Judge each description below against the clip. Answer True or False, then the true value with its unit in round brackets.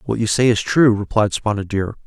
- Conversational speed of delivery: False (235 wpm)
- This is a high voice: False (110 Hz)